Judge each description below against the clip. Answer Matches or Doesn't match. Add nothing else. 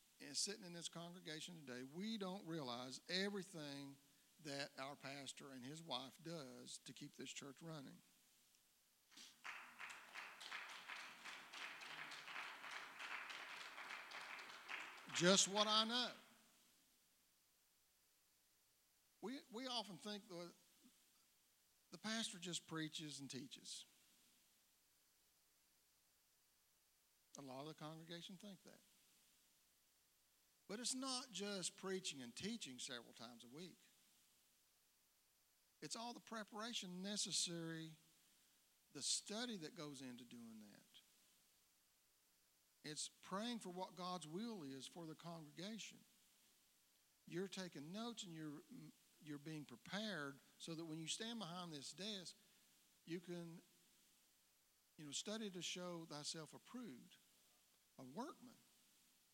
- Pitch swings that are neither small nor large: Doesn't match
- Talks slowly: Matches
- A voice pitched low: Doesn't match